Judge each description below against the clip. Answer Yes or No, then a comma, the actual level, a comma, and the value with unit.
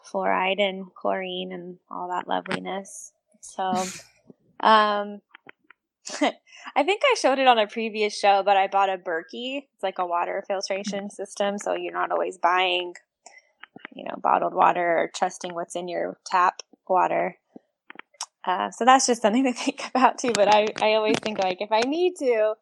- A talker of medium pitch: No, high, 205 Hz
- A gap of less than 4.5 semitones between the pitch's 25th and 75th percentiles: Yes, average, 3.7 semitones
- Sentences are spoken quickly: No, average, 170 wpm